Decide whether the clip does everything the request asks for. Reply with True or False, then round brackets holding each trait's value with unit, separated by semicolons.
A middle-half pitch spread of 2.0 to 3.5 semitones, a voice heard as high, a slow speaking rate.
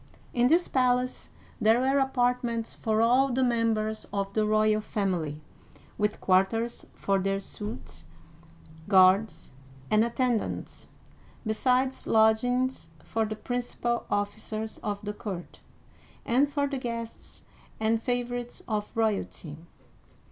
True (2.9 semitones; 225 Hz; 120 wpm)